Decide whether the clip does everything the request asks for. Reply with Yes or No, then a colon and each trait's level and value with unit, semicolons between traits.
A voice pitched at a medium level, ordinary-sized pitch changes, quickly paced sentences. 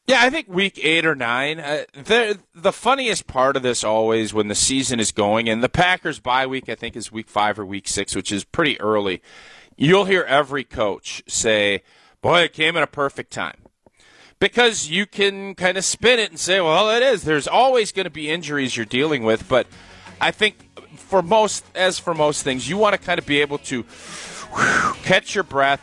No: medium, 145 Hz; wide, 8.9 semitones; fast, 210 wpm